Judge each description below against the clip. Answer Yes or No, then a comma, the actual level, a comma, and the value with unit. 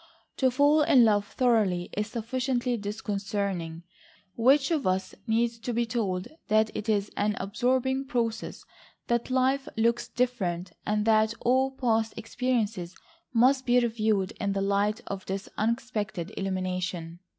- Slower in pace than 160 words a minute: Yes, average, 140 wpm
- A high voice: Yes, high, 220 Hz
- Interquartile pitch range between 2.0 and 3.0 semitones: No, average, 3.8 semitones